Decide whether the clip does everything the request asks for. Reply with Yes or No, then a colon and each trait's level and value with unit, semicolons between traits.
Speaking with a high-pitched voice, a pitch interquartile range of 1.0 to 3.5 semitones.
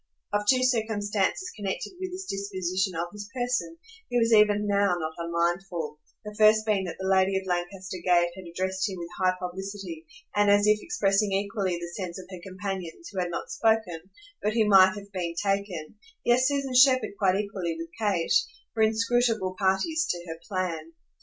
Yes: high, 195 Hz; average, 3.1 semitones